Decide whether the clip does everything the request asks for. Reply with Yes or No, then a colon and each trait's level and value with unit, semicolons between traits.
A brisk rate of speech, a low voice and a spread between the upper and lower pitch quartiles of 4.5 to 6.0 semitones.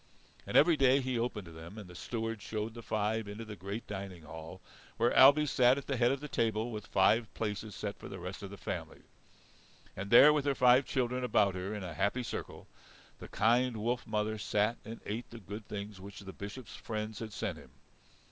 No: fast, 215 wpm; low, 110 Hz; average, 3.3 semitones